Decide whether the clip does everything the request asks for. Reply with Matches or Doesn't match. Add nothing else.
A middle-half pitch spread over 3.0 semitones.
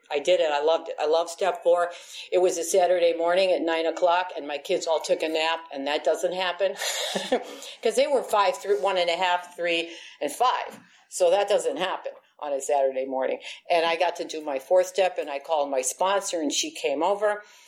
Doesn't match